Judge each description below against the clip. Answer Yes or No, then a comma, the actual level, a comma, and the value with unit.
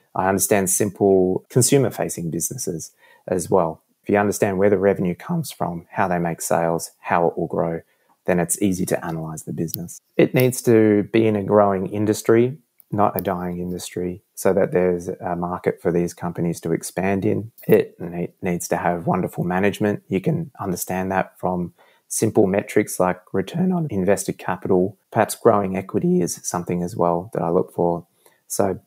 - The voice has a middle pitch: No, very low, 95 Hz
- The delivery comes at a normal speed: Yes, average, 175 wpm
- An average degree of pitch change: Yes, average, 3.3 semitones